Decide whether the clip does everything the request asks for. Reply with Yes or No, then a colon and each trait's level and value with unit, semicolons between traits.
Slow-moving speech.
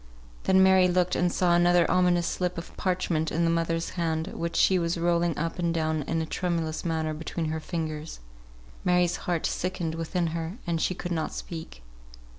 No: average, 185 wpm